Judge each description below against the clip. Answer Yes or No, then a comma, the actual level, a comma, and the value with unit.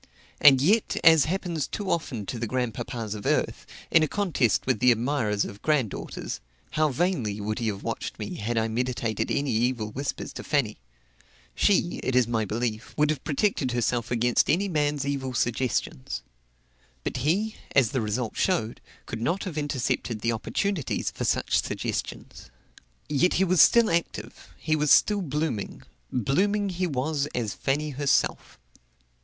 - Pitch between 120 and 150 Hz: Yes, low, 135 Hz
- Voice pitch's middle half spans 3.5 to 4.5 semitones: No, wide, 5.4 semitones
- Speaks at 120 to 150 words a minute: No, average, 160 wpm